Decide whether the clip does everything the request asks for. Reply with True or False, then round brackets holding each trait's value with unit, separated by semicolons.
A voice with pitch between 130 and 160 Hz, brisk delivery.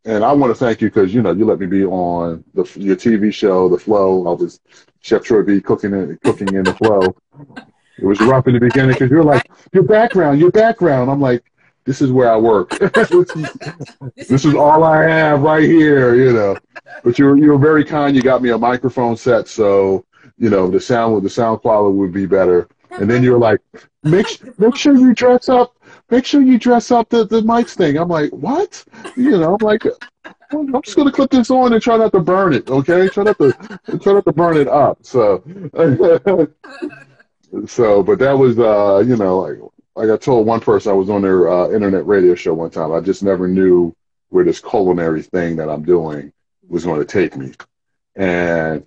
True (135 Hz; 210 wpm)